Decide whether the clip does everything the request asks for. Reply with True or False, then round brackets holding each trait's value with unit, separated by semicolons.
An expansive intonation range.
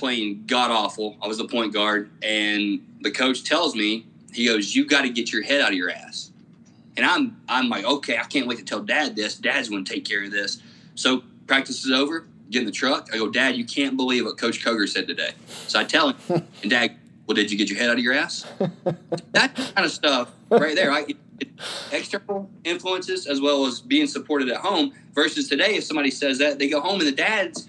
True (7.8 semitones)